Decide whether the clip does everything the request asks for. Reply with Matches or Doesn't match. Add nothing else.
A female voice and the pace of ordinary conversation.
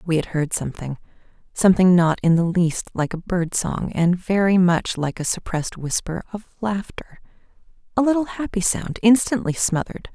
Matches